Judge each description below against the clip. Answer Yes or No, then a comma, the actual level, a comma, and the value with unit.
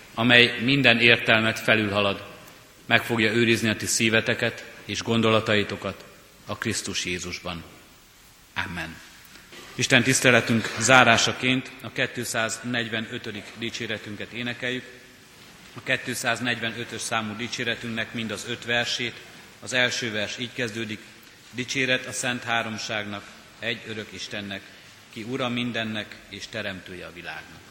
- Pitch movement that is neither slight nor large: No, narrow, 2.3 semitones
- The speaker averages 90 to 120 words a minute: Yes, average, 110 wpm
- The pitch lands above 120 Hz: No, low, 115 Hz